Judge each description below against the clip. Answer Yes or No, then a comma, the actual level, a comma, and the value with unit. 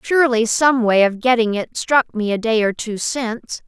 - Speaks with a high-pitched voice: Yes, high, 230 Hz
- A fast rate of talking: Yes, fast, 210 wpm